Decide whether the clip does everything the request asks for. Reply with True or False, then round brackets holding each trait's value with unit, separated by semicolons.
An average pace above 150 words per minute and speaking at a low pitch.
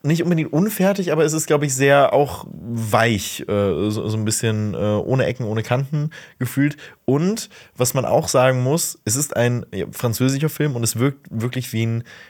True (175 wpm; 130 Hz)